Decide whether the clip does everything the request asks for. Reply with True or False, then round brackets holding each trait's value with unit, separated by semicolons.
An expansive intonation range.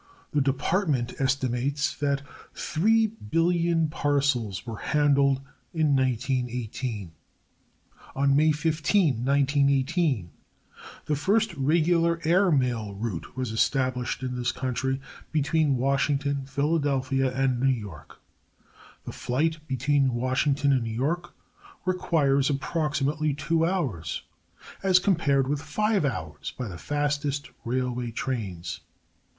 False (3.4 semitones)